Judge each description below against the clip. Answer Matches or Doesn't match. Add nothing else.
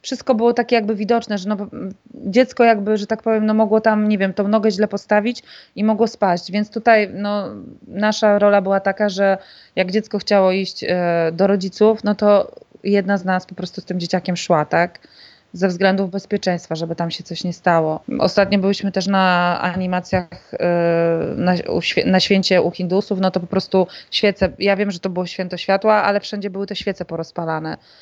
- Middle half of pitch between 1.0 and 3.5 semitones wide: Matches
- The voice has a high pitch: Matches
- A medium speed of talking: Doesn't match